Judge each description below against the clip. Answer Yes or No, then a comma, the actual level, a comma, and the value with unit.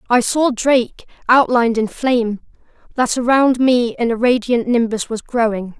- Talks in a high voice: Yes, high, 240 Hz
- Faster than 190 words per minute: No, average, 145 wpm